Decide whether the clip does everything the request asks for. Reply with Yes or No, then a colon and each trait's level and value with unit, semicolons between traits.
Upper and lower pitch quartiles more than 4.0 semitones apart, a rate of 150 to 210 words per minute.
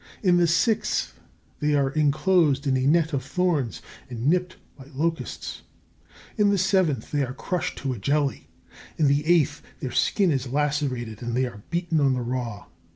Yes: average, 4.6 semitones; average, 175 wpm